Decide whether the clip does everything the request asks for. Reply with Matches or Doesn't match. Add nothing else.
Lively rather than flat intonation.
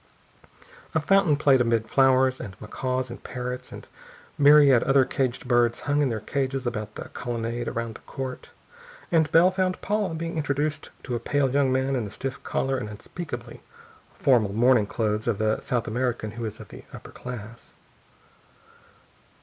Doesn't match